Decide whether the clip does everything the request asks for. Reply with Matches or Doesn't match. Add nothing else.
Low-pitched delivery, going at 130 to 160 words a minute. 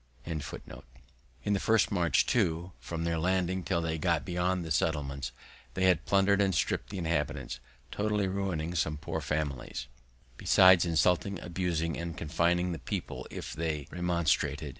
Matches